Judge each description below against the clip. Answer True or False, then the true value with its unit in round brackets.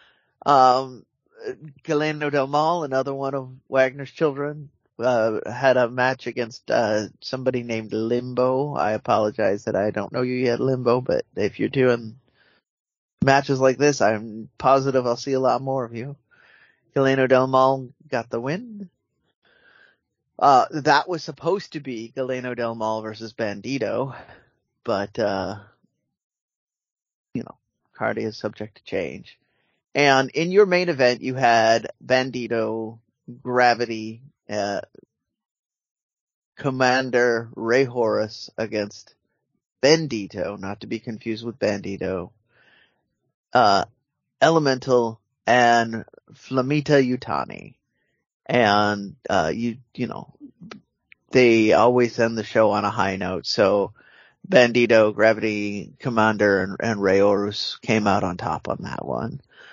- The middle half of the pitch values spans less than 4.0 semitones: True (3.4 semitones)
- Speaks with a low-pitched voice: True (120 Hz)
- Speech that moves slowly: True (125 wpm)